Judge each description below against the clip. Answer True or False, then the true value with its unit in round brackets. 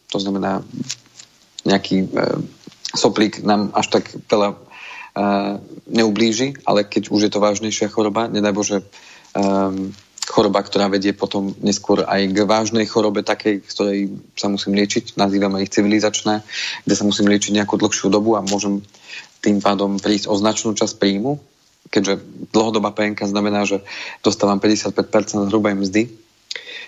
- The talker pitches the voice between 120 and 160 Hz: False (105 Hz)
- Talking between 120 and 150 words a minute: True (140 wpm)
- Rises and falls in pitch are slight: True (1.2 semitones)